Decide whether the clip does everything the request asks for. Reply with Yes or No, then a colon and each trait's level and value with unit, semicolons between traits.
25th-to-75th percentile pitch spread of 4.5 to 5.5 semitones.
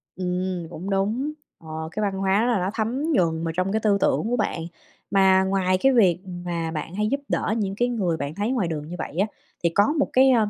No: average, 4.1 semitones